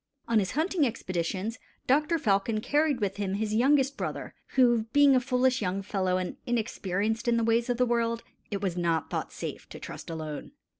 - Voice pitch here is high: Yes, high, 230 Hz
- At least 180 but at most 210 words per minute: Yes, average, 190 wpm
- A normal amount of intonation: Yes, average, 4.5 semitones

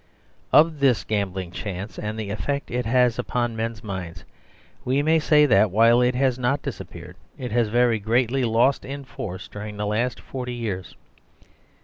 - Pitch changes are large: No, average, 3.5 semitones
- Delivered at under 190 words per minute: Yes, average, 170 wpm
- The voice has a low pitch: Yes, low, 115 Hz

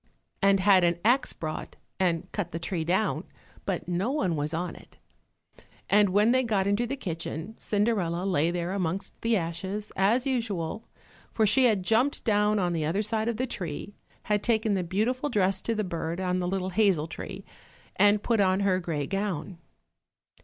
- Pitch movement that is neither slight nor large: Yes, average, 3.8 semitones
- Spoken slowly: No, average, 180 wpm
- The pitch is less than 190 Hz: No, high, 195 Hz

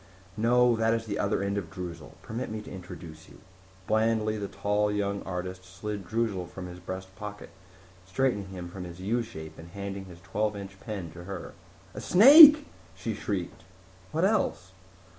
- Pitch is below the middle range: Yes, low, 100 Hz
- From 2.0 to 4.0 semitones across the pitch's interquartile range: Yes, average, 3.1 semitones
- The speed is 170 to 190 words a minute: Yes, average, 175 wpm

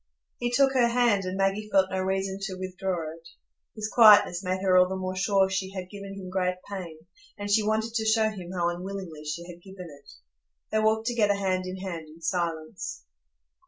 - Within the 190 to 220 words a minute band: Yes, average, 200 wpm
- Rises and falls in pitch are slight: Yes, narrow, 2.2 semitones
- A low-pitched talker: No, high, 190 Hz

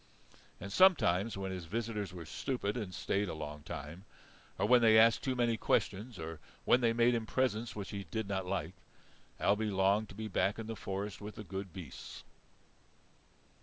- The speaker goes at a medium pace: Yes, average, 185 wpm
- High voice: No, low, 105 Hz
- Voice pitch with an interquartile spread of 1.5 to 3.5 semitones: Yes, average, 3.2 semitones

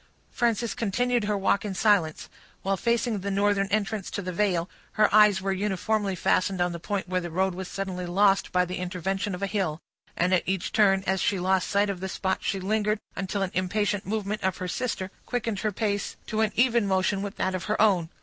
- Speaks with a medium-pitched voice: No, high, 195 Hz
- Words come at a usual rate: No, fast, 215 wpm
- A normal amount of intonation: No, narrow, 2.2 semitones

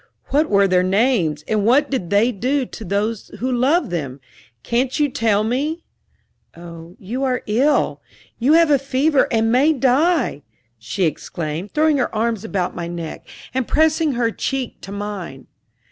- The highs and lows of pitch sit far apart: Yes, wide, 6.1 semitones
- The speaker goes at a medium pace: Yes, average, 160 wpm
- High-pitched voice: Yes, high, 230 Hz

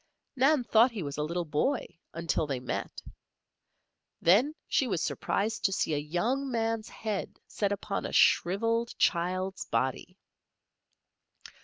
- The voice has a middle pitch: No, high, 200 Hz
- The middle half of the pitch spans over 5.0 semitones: Yes, wide, 5.4 semitones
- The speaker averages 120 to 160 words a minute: Yes, slow, 135 wpm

